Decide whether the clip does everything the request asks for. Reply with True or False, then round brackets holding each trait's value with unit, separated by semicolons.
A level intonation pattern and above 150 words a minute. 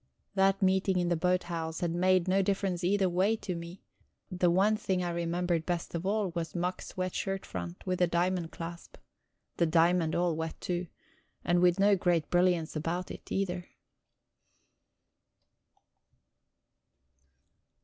False (1.7 semitones; 140 wpm)